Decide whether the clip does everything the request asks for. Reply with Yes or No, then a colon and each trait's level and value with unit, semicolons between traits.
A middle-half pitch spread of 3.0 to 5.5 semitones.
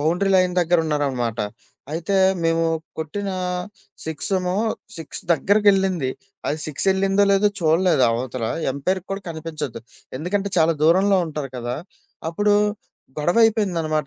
Yes: average, 4.2 semitones